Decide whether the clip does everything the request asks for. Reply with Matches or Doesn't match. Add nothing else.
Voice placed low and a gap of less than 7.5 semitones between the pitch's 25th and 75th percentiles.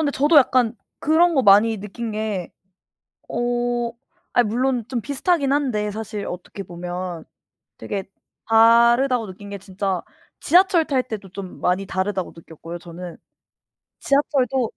Doesn't match